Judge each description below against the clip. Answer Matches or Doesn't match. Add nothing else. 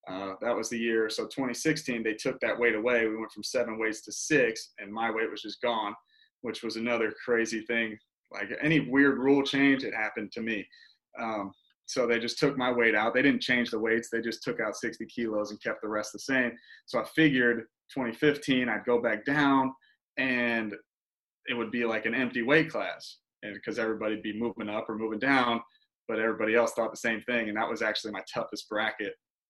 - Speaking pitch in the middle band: Doesn't match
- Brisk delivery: Matches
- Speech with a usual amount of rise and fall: Matches